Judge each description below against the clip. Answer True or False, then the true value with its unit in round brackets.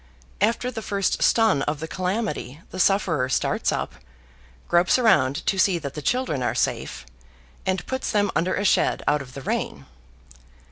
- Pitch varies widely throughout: True (6.0 semitones)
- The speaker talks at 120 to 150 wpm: False (170 wpm)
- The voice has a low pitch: False (185 Hz)